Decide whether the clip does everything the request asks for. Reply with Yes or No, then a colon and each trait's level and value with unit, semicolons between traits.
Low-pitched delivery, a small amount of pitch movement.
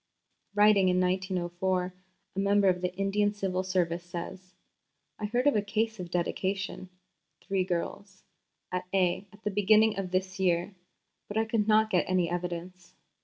No: high, 190 Hz; narrow, 2.2 semitones